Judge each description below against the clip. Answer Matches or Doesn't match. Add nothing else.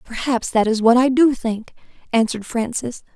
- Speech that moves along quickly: Doesn't match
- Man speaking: Doesn't match